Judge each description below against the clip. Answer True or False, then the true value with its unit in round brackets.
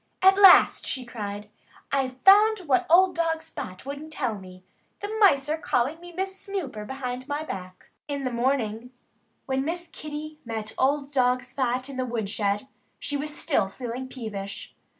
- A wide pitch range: False (4.8 semitones)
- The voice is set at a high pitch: True (265 Hz)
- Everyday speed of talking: True (170 wpm)